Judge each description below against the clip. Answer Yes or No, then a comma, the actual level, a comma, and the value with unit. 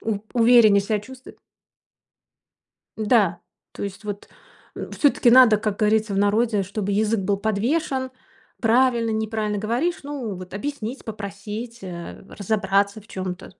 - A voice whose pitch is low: No, high, 215 Hz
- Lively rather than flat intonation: No, average, 2.8 semitones